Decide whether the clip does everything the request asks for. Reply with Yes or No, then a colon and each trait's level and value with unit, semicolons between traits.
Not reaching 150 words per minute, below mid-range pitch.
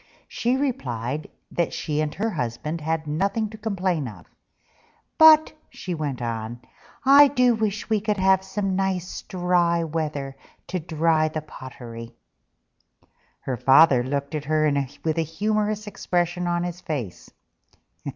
No: average, 140 wpm; medium, 165 Hz